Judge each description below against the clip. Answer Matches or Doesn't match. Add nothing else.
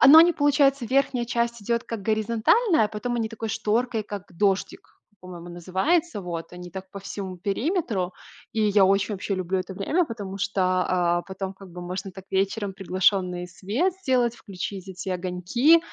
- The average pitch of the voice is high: Matches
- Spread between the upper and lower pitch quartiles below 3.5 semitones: Doesn't match